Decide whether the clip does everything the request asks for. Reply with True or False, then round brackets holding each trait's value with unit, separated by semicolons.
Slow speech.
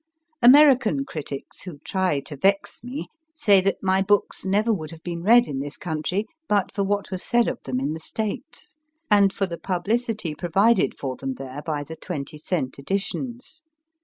False (180 wpm)